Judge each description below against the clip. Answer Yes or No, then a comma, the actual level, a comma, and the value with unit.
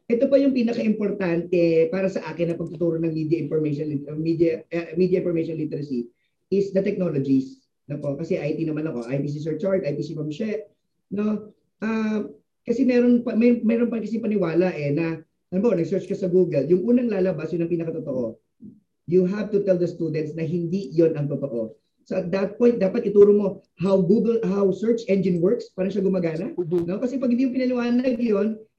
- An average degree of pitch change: Yes, average, 4.6 semitones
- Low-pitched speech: No, medium, 185 Hz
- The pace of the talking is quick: Yes, fast, 180 wpm